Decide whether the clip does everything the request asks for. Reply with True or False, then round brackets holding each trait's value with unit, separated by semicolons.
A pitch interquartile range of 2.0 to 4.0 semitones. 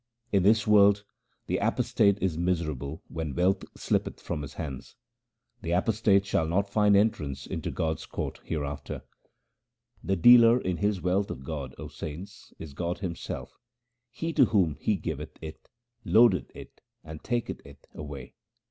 False (4.6 semitones)